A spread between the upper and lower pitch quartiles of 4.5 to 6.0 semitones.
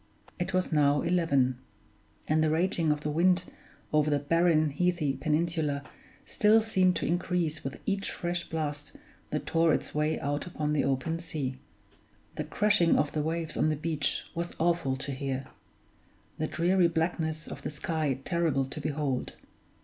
No: average, 2.9 semitones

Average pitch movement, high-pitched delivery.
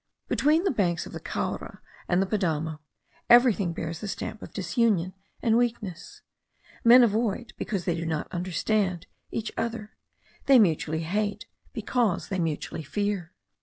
Yes: average, 4.9 semitones; high, 200 Hz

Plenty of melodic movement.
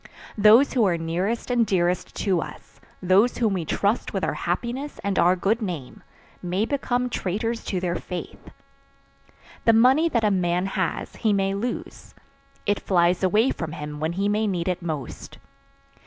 No: average, 4.4 semitones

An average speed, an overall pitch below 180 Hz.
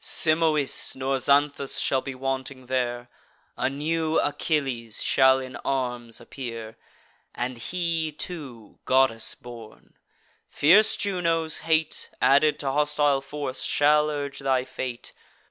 No: slow, 115 wpm; low, 135 Hz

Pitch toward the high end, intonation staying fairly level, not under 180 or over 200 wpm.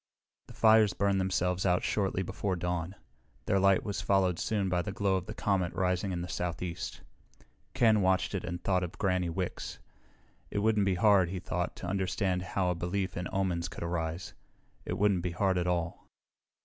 No: very low, 95 Hz; narrow, 1.8 semitones; average, 190 wpm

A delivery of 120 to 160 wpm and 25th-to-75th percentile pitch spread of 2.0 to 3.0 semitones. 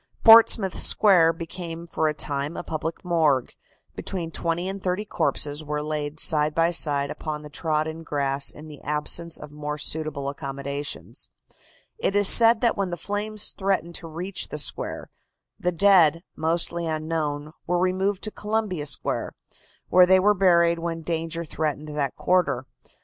No: average, 155 wpm; average, 3.4 semitones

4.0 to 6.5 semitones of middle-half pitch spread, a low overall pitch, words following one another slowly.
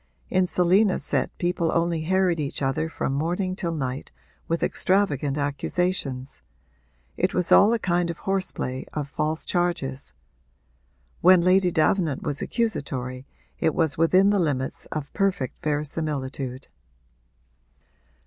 No: average, 4.5 semitones; medium, 165 Hz; slow, 130 wpm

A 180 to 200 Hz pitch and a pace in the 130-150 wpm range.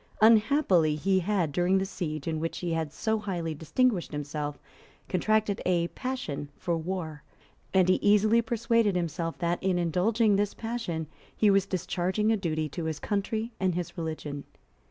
No: medium, 185 Hz; average, 160 wpm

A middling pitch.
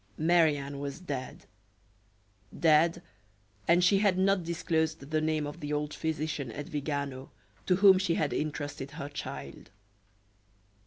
Yes: medium, 155 Hz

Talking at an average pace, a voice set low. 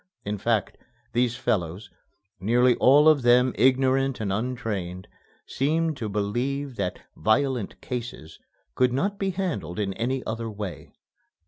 No: slow, 130 wpm; low, 120 Hz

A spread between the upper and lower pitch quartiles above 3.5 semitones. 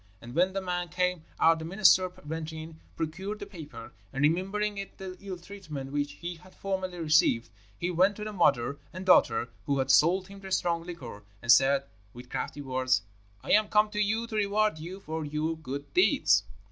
Yes: average, 4.7 semitones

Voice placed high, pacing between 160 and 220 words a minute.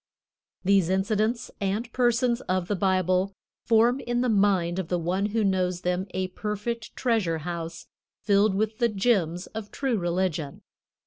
No: high, 195 Hz; average, 150 wpm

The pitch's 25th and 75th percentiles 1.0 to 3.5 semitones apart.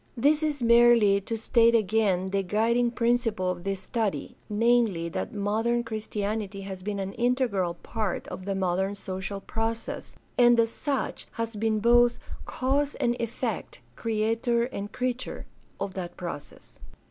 Yes: average, 3.2 semitones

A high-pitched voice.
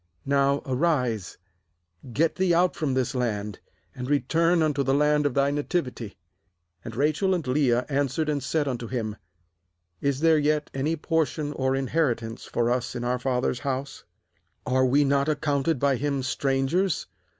No: medium, 140 Hz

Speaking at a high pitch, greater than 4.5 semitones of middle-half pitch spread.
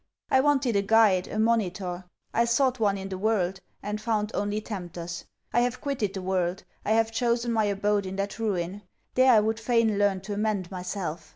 No: high, 210 Hz; average, 3.0 semitones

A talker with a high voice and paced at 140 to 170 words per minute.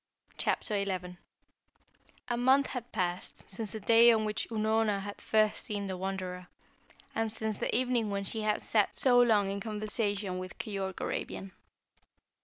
Yes: high, 210 Hz; average, 155 wpm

